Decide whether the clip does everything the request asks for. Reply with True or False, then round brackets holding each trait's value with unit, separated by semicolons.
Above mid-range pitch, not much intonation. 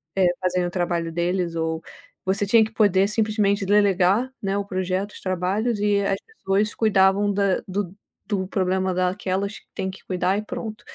True (195 Hz; 1.9 semitones)